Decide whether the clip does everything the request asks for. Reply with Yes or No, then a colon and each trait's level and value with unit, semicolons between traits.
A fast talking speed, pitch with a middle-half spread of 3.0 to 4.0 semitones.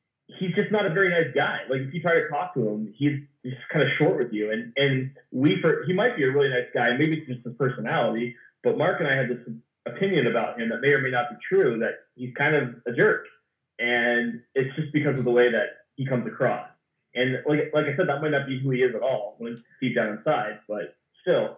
Yes: fast, 255 wpm; average, 3.7 semitones